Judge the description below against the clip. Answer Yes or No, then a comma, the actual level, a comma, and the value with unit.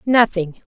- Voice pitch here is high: Yes, high, 205 Hz